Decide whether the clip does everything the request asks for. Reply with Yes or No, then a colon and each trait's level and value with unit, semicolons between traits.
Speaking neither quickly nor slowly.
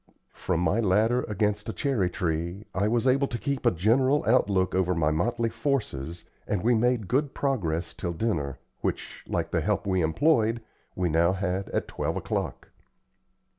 Yes: average, 170 wpm